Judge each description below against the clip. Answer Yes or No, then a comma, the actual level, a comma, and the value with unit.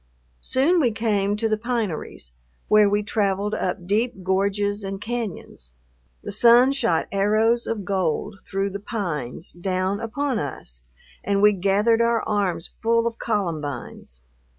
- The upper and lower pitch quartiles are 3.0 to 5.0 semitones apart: Yes, average, 3.3 semitones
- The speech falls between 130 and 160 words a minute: Yes, average, 140 wpm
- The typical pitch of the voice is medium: No, high, 205 Hz